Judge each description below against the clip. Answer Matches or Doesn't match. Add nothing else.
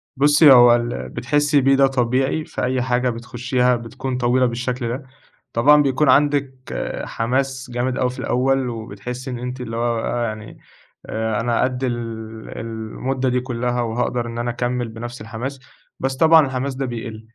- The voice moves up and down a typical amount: Doesn't match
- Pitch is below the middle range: Matches